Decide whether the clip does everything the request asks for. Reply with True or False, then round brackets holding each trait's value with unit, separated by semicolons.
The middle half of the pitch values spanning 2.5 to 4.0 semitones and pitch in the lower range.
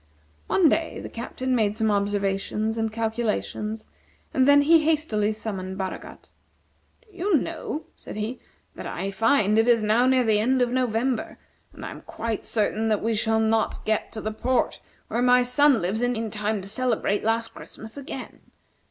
False (3.1 semitones; 225 Hz)